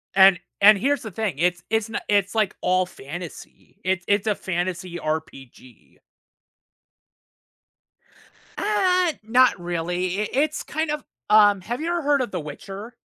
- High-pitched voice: Yes, high, 200 Hz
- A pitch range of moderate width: No, wide, 5.7 semitones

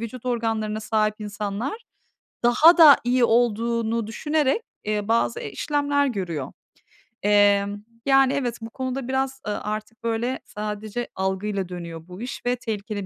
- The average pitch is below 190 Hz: No, high, 225 Hz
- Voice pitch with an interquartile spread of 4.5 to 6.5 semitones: No, average, 3.5 semitones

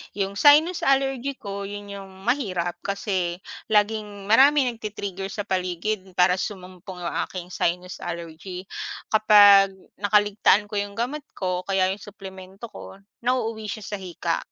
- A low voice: No, high, 200 Hz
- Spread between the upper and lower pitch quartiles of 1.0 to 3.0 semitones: Yes, average, 2.7 semitones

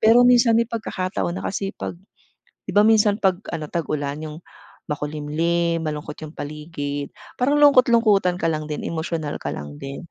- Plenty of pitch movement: Yes, wide, 6.0 semitones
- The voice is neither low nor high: Yes, medium, 165 Hz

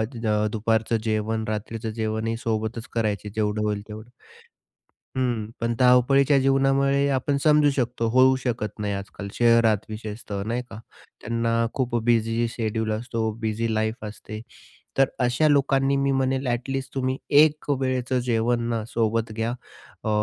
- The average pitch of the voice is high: No, low, 115 Hz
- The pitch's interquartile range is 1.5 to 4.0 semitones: Yes, average, 2.9 semitones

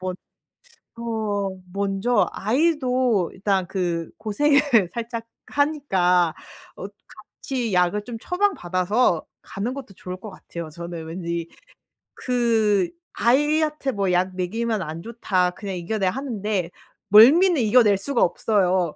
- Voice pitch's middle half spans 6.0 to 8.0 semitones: No, average, 5.2 semitones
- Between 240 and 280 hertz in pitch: No, high, 205 Hz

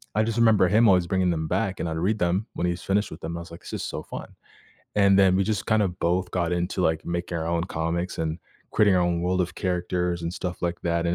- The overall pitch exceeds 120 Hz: No, very low, 90 Hz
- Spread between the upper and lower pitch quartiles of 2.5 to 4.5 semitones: No, narrow, 2.1 semitones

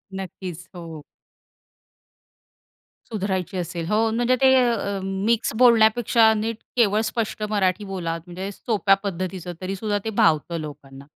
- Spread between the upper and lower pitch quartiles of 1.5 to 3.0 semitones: No, average, 3.8 semitones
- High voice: Yes, high, 195 Hz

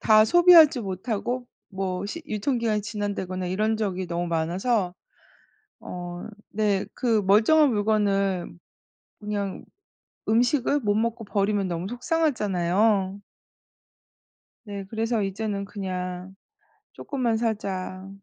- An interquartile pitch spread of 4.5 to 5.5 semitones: No, average, 3.2 semitones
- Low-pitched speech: No, high, 205 Hz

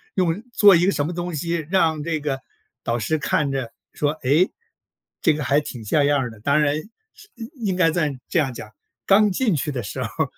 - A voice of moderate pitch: Yes, medium, 155 Hz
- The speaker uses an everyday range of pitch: Yes, average, 4.1 semitones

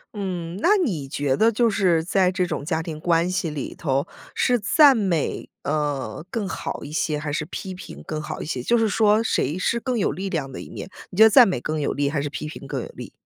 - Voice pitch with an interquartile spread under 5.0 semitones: No, wide, 5.6 semitones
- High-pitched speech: No, medium, 170 Hz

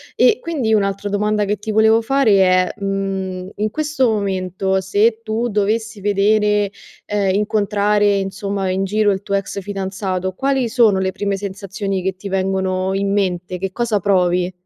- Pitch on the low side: No, high, 200 Hz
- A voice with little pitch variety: Yes, narrow, 1.9 semitones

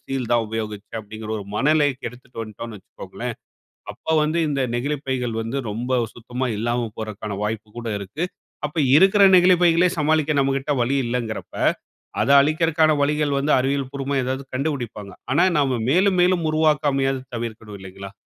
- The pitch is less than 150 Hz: Yes, low, 135 Hz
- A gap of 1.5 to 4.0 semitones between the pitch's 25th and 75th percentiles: No, average, 4.8 semitones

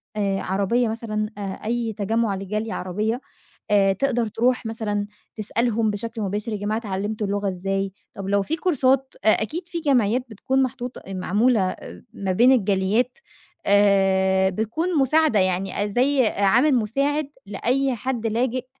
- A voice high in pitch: Yes, high, 220 Hz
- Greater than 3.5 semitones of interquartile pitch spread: Yes, average, 4.0 semitones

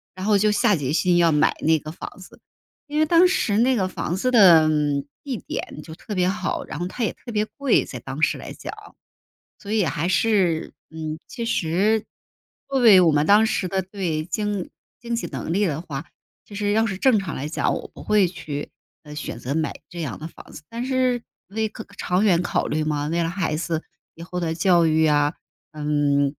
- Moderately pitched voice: Yes, medium, 180 Hz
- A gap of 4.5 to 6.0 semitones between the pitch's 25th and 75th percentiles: Yes, average, 5.2 semitones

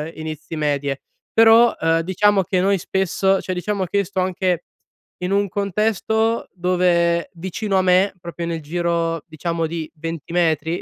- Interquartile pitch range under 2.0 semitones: No, average, 2.8 semitones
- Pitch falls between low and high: Yes, medium, 175 Hz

